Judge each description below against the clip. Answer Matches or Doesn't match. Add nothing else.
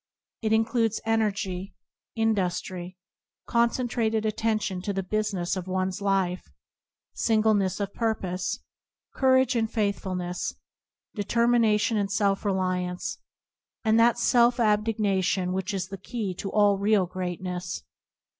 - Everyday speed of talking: Doesn't match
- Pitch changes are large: Doesn't match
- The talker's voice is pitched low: Doesn't match